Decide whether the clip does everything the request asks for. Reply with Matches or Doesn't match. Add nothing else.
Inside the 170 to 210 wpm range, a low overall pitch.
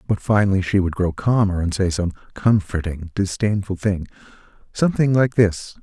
Doesn't match